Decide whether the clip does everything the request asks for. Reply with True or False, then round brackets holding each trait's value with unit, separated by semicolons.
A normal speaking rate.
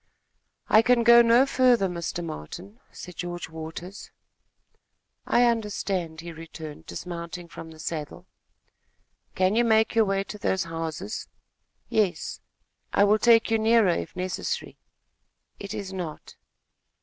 False (130 wpm)